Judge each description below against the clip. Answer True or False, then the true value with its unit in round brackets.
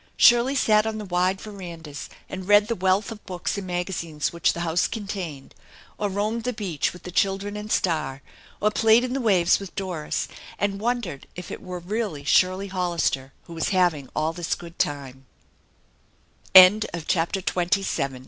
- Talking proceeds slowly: False (160 wpm)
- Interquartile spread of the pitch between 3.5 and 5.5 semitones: True (3.8 semitones)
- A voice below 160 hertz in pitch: False (185 Hz)